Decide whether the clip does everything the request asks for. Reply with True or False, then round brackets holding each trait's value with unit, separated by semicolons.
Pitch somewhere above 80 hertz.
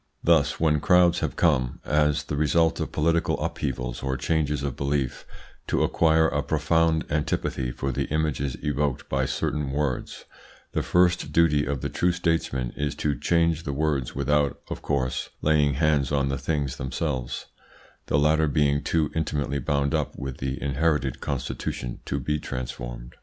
False (75 Hz)